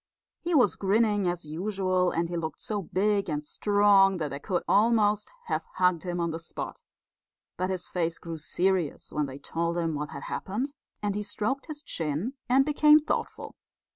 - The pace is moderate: Yes, average, 180 wpm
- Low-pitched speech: No, medium, 185 Hz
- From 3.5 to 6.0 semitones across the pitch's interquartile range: Yes, average, 3.9 semitones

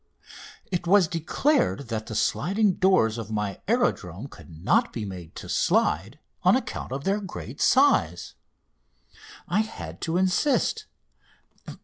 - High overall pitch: No, medium, 140 Hz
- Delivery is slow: Yes, slow, 130 wpm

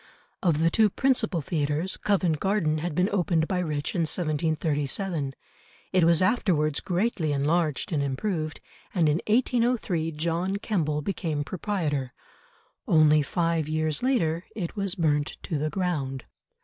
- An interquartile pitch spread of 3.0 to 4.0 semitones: Yes, average, 3.7 semitones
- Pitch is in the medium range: Yes, medium, 165 Hz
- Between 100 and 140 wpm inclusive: Yes, slow, 135 wpm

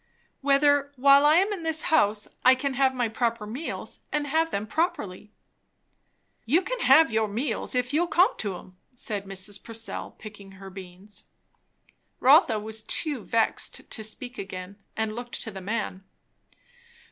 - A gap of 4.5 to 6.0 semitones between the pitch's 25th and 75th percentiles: Yes, wide, 5.6 semitones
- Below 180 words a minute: Yes, average, 160 wpm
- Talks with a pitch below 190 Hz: No, high, 230 Hz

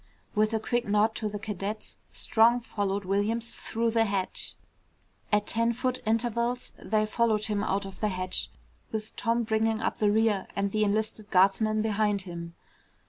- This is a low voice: No, high, 215 Hz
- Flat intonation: Yes, narrow, 1.9 semitones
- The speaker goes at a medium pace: Yes, average, 165 wpm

